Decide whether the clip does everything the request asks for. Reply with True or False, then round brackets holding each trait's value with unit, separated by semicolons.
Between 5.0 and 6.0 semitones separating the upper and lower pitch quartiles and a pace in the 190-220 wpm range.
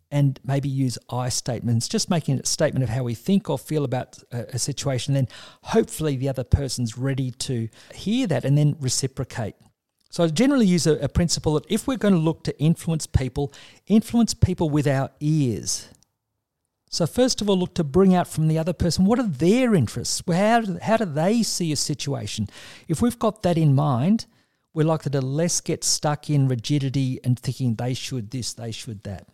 True (5.5 semitones; 200 wpm)